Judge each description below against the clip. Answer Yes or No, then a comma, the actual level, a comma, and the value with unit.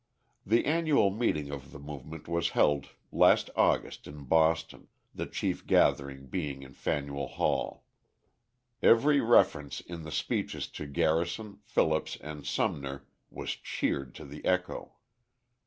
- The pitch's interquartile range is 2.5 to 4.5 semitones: Yes, average, 3.9 semitones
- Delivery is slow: Yes, slow, 130 wpm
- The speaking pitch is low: Yes, very low, 75 Hz